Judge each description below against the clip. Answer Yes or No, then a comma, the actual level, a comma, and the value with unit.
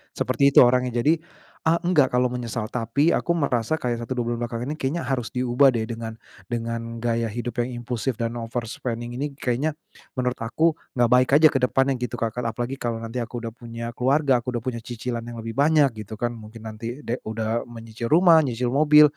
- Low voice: Yes, low, 120 Hz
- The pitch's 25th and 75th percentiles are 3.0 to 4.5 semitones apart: No, narrow, 2.4 semitones